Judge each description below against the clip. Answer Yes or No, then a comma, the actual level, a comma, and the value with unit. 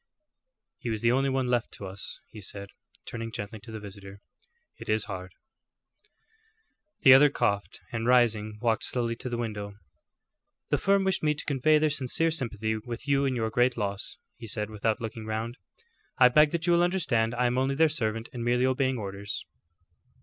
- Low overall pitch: Yes, low, 120 Hz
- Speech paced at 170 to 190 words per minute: Yes, average, 185 wpm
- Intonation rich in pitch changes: No, average, 3.6 semitones